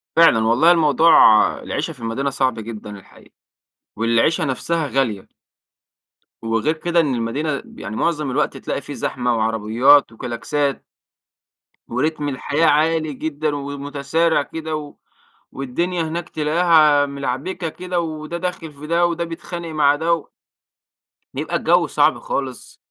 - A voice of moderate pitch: Yes, medium, 145 Hz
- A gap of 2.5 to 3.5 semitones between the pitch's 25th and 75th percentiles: No, average, 4.2 semitones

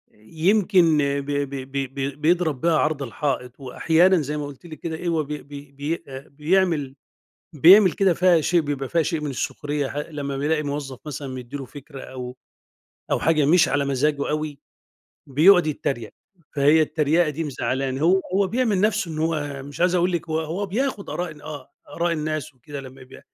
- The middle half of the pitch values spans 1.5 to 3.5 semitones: Yes, average, 3.2 semitones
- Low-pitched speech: No, medium, 150 Hz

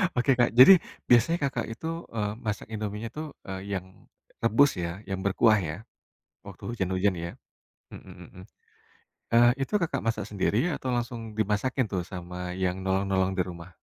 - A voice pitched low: Yes, low, 105 Hz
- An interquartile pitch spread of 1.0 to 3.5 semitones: No, average, 4.2 semitones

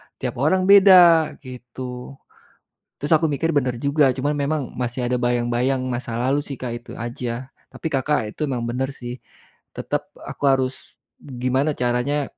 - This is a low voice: Yes, low, 130 Hz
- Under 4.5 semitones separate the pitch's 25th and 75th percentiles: Yes, average, 2.9 semitones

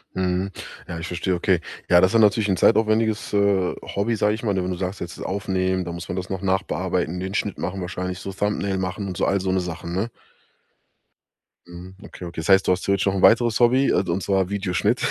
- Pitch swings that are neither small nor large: No, narrow, 2.0 semitones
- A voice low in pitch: Yes, very low, 95 Hz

